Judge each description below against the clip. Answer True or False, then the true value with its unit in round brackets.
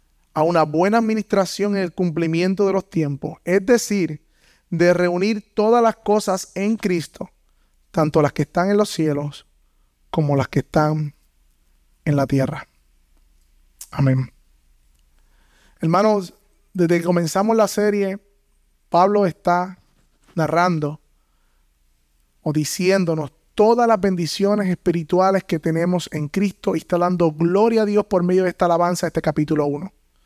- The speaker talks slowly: False (135 wpm)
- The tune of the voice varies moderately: False (6.0 semitones)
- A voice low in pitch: False (170 Hz)